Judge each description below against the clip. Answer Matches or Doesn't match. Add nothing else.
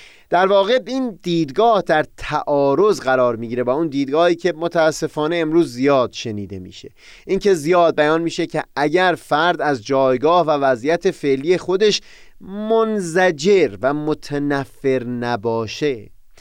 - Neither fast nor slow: Matches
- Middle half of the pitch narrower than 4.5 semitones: Doesn't match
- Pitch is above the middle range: Doesn't match